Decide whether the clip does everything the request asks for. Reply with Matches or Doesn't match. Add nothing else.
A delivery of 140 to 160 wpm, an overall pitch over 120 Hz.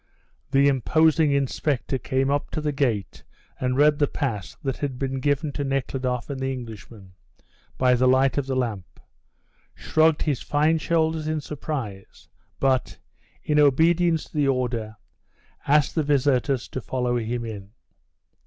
Matches